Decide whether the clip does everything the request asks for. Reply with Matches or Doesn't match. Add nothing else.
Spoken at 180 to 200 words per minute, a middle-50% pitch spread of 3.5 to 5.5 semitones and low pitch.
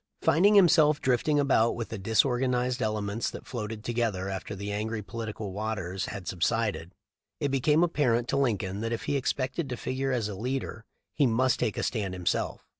Matches